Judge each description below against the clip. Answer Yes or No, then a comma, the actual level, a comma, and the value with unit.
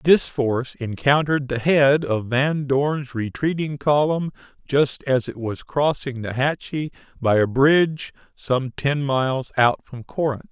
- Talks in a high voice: No, low, 135 Hz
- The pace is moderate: Yes, average, 150 wpm